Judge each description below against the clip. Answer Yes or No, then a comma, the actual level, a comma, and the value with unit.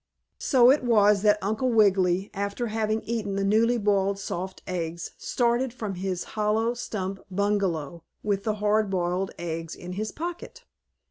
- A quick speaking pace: No, average, 150 wpm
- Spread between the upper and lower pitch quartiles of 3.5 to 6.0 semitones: No, average, 2.9 semitones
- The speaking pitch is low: No, high, 205 Hz